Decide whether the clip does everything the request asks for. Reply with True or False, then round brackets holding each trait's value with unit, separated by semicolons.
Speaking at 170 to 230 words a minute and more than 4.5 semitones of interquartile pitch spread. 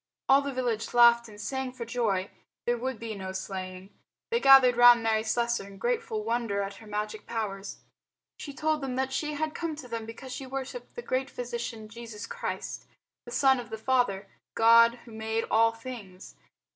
False (185 wpm; 3.3 semitones)